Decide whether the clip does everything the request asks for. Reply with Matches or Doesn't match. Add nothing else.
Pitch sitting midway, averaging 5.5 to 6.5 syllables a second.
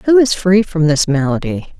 Doesn't match